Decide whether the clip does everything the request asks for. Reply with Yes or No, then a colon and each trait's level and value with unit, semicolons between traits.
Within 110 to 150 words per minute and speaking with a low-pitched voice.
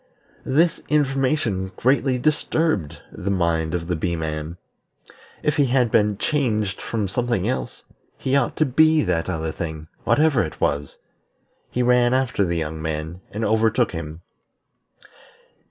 Yes: average, 140 wpm; low, 105 Hz